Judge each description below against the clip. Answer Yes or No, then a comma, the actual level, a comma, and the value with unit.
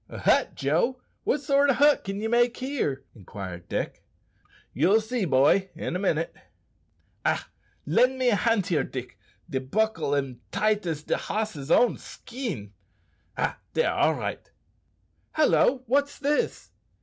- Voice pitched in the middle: No, high, 210 Hz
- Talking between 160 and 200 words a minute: No, average, 150 wpm